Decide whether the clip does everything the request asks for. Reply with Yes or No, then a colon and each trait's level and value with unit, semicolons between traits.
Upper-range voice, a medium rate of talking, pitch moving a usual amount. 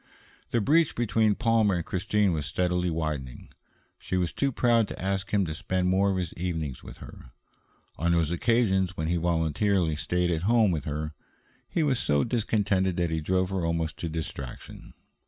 No: very low, 90 Hz; average, 180 wpm; average, 4.1 semitones